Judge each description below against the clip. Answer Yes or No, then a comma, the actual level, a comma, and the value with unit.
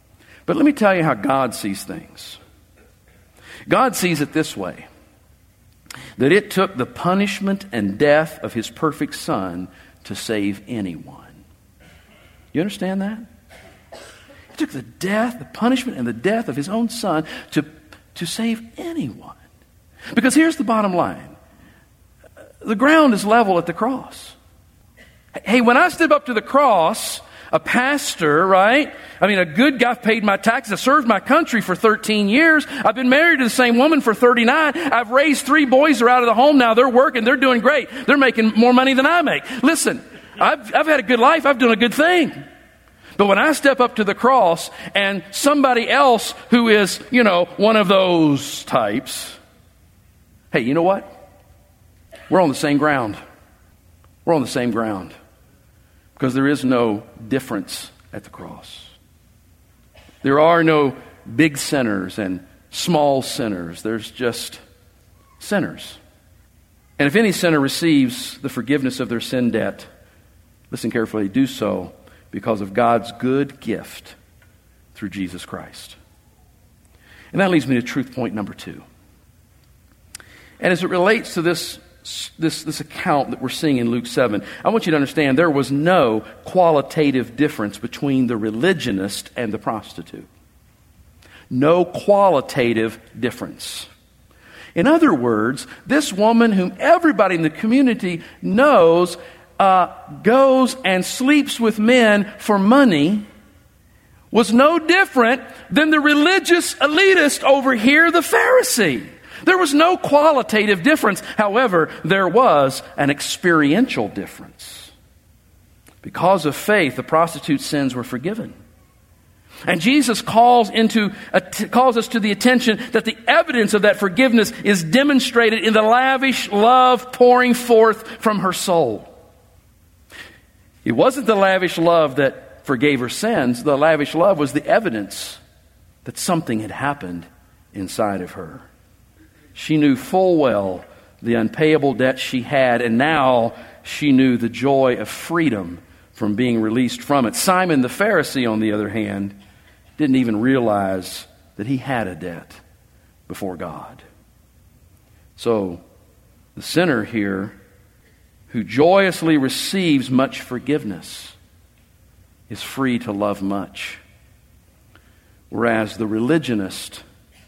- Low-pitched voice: No, medium, 155 Hz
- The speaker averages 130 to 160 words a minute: Yes, average, 145 wpm